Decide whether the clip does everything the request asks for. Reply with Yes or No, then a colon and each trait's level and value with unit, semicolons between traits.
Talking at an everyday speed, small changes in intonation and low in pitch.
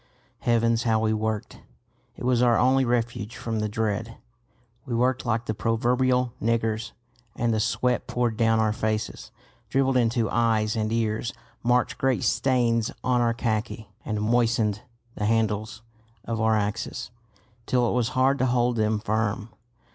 Yes: average, 155 wpm; narrow, 1.9 semitones; low, 115 Hz